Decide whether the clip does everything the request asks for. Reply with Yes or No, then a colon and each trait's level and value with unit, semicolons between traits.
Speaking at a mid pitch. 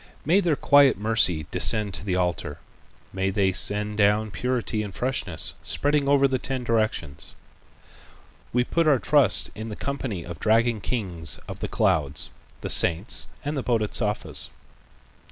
No: low, 110 Hz